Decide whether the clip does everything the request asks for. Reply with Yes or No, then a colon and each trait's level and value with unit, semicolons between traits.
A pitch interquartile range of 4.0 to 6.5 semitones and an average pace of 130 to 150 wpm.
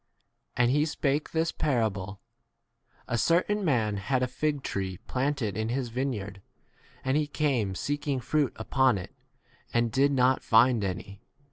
Yes: average, 4.8 semitones; average, 145 wpm